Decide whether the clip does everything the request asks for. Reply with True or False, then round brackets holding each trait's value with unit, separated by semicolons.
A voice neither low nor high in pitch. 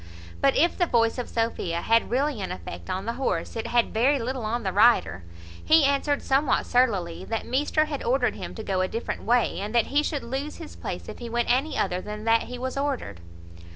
False (240 Hz)